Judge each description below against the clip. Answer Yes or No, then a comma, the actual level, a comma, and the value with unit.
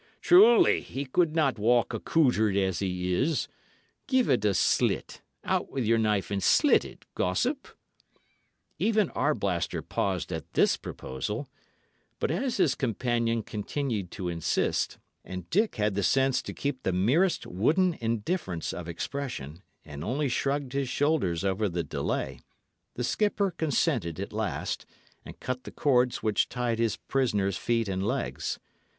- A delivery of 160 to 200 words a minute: No, average, 145 wpm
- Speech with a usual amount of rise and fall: No, wide, 6.8 semitones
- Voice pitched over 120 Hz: No, low, 115 Hz